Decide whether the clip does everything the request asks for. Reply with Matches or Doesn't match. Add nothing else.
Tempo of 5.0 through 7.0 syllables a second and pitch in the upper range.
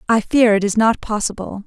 Matches